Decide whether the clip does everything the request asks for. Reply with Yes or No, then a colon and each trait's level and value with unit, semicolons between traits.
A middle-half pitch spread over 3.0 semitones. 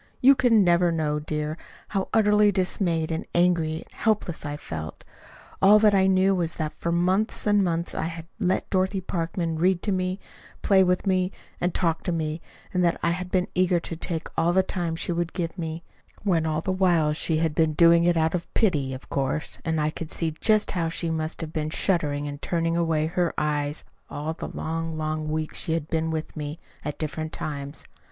No: average, 2.7 semitones